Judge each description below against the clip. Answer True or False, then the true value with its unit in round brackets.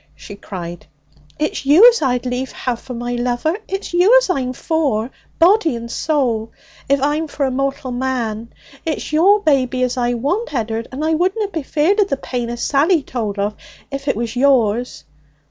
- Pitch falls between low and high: False (265 Hz)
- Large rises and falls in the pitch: False (4.8 semitones)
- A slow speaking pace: False (185 wpm)